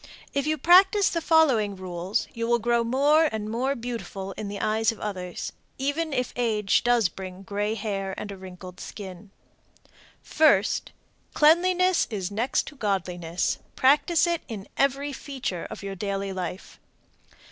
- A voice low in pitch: No, high, 220 Hz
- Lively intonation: Yes, wide, 6.2 semitones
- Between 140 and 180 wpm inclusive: Yes, average, 155 wpm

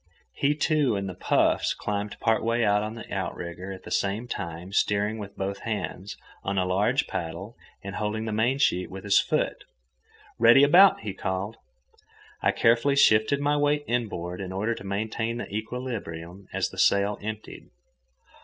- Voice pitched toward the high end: No, low, 105 Hz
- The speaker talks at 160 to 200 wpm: Yes, average, 165 wpm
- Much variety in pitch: No, average, 3.3 semitones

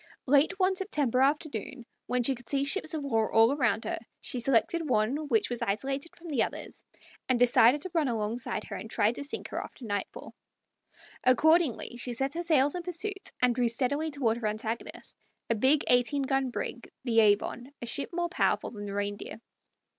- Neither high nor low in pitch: No, very high, 260 Hz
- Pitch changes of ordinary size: Yes, average, 4.6 semitones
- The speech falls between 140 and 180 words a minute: No, average, 190 wpm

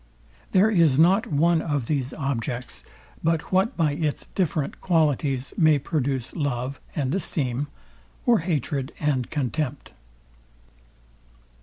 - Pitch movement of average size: Yes, average, 3.7 semitones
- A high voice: No, medium, 150 Hz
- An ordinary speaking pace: No, slow, 115 wpm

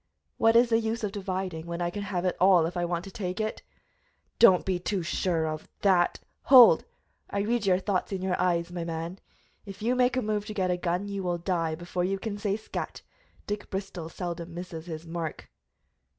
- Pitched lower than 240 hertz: Yes, medium, 185 Hz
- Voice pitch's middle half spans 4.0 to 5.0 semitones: No, average, 2.9 semitones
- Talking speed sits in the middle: No, fast, 220 wpm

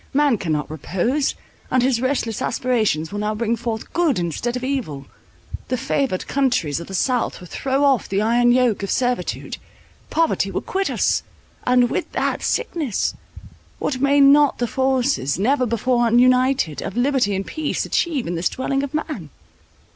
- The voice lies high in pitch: Yes, high, 245 Hz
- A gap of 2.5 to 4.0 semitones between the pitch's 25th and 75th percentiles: No, average, 4.8 semitones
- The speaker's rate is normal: Yes, average, 165 wpm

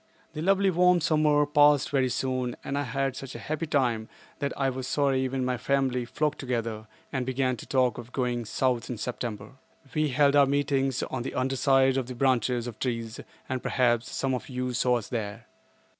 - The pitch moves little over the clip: Yes, narrow, 2.3 semitones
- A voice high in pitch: No, low, 130 Hz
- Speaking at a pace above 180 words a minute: Yes, average, 195 wpm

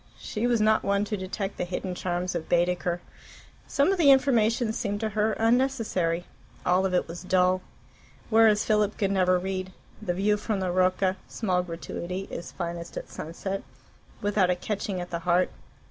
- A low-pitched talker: No, high, 190 Hz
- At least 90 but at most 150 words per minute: No, average, 175 wpm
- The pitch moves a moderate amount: Yes, average, 3.0 semitones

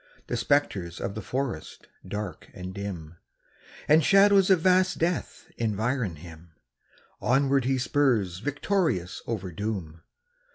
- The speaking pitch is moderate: No, low, 110 Hz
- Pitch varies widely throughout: Yes, wide, 7.9 semitones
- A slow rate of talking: Yes, slow, 120 wpm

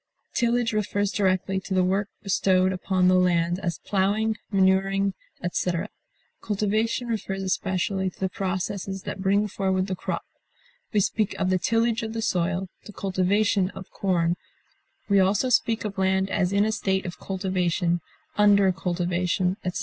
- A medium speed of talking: Yes, average, 155 wpm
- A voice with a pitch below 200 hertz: Yes, high, 190 Hz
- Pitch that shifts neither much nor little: No, narrow, 1.8 semitones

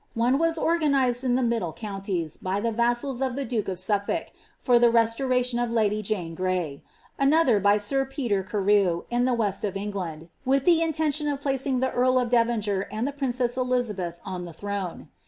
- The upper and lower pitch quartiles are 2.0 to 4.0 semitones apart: No, average, 4.7 semitones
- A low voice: No, high, 235 Hz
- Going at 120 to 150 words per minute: No, average, 195 wpm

